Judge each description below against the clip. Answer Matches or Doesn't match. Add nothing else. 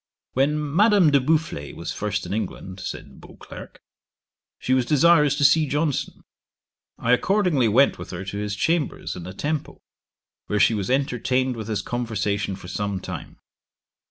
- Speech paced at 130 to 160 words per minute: Matches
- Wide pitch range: Matches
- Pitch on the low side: Matches